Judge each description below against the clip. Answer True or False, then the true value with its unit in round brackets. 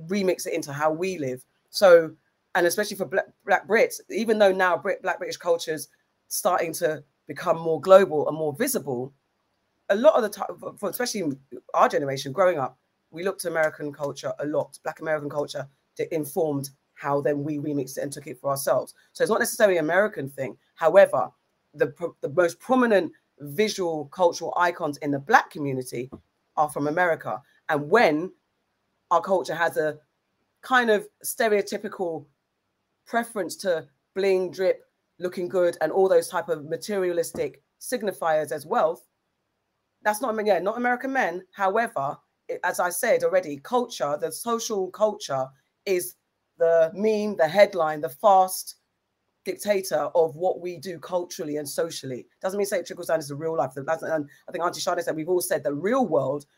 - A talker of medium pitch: True (175 Hz)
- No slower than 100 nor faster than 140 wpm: False (175 wpm)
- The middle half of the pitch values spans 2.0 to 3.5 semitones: False (4.9 semitones)